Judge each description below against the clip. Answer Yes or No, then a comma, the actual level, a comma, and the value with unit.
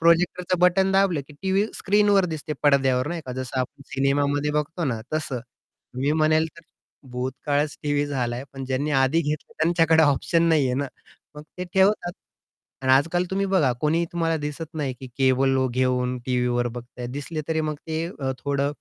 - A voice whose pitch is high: No, medium, 150 Hz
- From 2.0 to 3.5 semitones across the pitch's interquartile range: No, average, 4.0 semitones